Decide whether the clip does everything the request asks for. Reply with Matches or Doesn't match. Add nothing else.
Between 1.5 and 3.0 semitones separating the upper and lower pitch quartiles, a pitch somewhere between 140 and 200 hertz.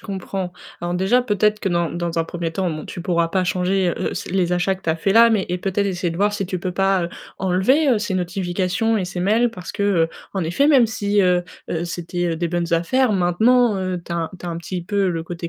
Matches